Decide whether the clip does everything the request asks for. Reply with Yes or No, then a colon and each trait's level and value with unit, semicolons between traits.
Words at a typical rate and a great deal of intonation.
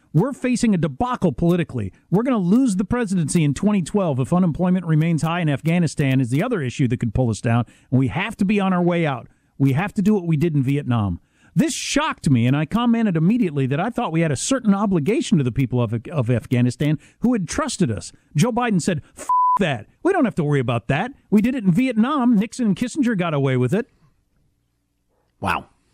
No: fast, 220 wpm; wide, 8.0 semitones